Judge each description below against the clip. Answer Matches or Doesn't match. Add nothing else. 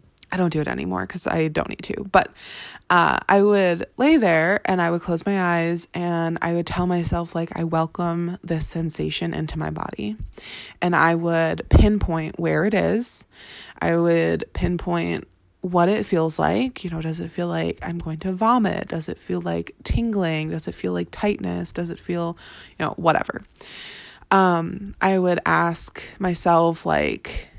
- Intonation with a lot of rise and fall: Doesn't match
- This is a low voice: Doesn't match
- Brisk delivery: Doesn't match